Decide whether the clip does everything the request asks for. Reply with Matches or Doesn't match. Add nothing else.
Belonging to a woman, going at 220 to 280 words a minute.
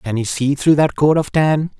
Doesn't match